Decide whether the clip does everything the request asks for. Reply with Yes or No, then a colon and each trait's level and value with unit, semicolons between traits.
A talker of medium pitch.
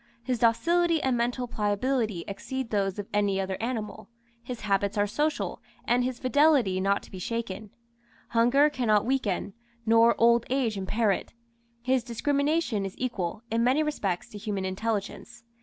No: high, 230 Hz